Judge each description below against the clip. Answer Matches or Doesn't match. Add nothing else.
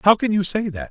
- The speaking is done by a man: Matches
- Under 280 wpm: Doesn't match